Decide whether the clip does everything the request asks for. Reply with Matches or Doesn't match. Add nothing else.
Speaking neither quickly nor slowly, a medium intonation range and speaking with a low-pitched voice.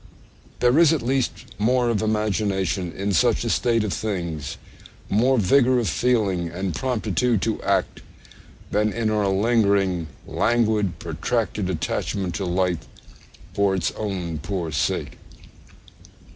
Doesn't match